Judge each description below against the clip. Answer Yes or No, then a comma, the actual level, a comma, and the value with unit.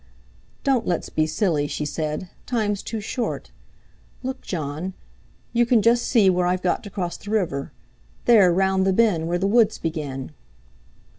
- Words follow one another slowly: No, average, 160 wpm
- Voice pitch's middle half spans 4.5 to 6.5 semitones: Yes, average, 5.2 semitones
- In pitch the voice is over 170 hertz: Yes, high, 190 Hz